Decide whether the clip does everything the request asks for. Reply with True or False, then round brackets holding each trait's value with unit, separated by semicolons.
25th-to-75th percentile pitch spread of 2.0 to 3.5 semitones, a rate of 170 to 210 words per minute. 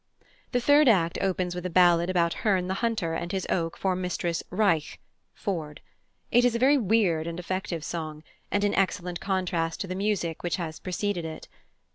True (3.2 semitones; 185 wpm)